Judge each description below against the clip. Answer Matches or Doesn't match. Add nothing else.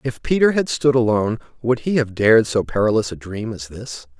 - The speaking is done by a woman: Doesn't match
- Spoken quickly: Matches